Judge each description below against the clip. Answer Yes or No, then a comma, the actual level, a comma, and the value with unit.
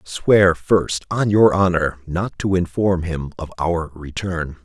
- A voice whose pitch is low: Yes, very low, 90 Hz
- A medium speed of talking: Yes, average, 155 wpm